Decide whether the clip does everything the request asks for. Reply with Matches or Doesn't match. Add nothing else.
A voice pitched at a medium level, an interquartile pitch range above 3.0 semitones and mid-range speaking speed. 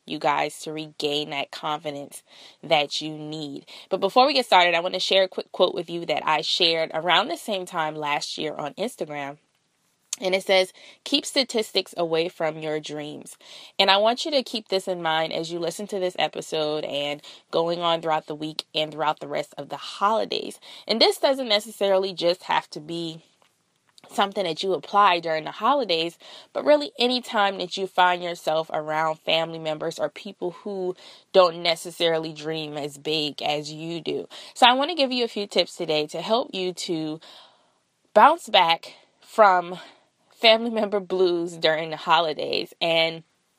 Matches